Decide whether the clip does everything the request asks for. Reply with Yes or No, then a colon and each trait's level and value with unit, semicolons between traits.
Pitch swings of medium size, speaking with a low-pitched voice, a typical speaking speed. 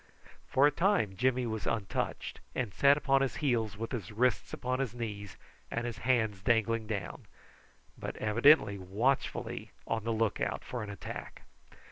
Yes: average, 3.3 semitones; low, 115 Hz; average, 160 wpm